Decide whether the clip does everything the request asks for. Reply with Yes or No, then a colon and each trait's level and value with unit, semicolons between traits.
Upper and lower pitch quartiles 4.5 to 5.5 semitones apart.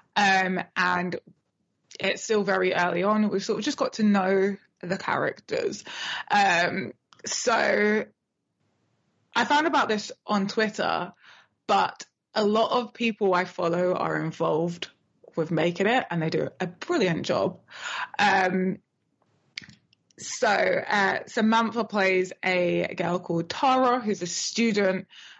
No: average, 4.0 semitones